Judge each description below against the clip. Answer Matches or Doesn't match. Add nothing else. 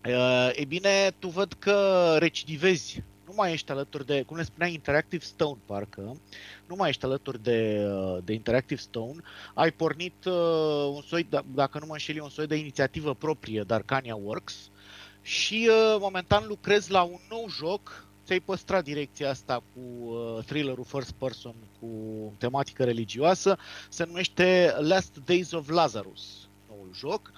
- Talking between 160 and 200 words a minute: Doesn't match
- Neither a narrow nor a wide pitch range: Doesn't match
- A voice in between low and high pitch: Matches